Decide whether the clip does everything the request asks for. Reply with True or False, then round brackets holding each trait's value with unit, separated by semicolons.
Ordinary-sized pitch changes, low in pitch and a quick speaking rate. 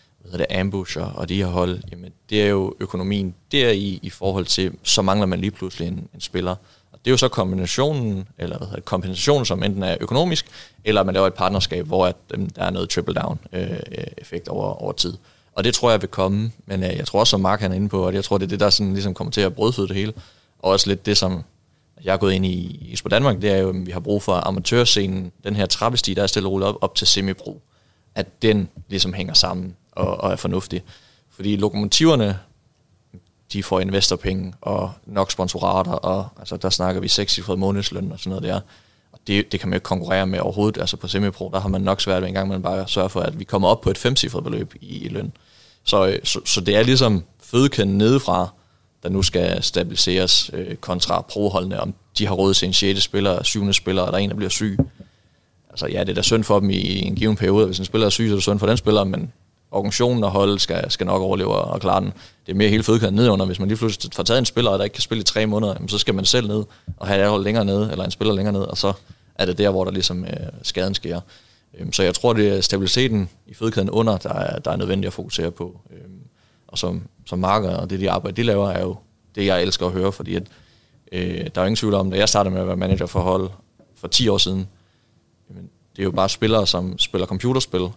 False (2.3 semitones; 95 Hz; 250 wpm)